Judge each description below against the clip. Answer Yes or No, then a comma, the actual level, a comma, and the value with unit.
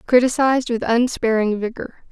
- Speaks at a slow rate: Yes, slow, 115 wpm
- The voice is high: Yes, high, 235 Hz